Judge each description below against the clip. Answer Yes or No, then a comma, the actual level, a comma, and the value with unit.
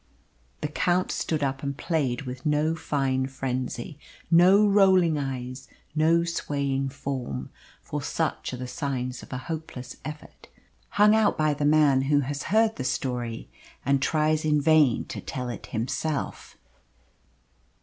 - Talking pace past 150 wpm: No, average, 145 wpm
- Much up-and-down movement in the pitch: No, average, 3.4 semitones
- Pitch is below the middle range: No, medium, 145 Hz